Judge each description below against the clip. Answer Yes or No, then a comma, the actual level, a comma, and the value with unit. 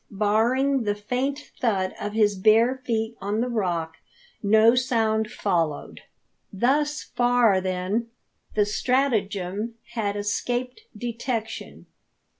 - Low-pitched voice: No, high, 220 Hz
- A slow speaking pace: Yes, slow, 105 wpm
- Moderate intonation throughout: Yes, average, 3.2 semitones